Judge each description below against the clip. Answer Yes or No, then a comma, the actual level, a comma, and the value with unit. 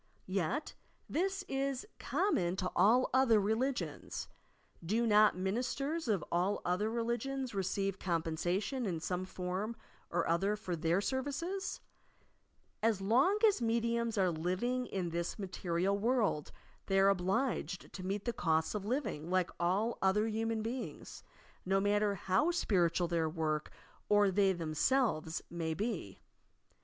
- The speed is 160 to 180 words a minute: No, average, 140 wpm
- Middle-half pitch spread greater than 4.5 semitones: Yes, average, 4.9 semitones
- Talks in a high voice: Yes, high, 200 Hz